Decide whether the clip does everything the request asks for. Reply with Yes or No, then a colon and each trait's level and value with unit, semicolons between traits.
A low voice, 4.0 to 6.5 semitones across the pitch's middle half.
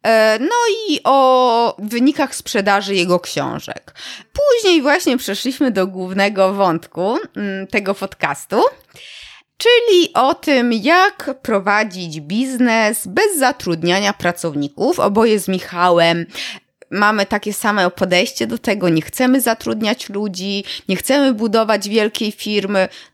No: high, 210 Hz; average, 5.1 semitones